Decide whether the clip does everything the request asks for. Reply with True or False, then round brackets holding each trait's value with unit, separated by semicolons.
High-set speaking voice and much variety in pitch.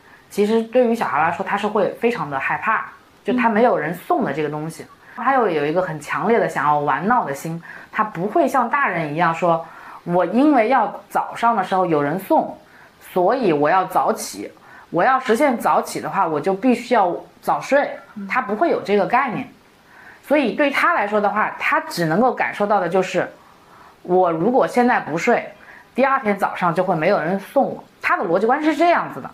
True (210 Hz; 6.1 semitones)